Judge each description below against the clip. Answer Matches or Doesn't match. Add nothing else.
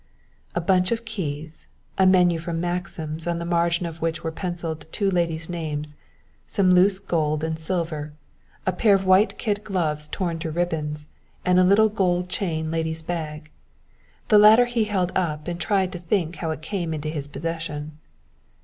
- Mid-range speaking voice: Matches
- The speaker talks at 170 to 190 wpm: Matches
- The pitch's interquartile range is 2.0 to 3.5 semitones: Matches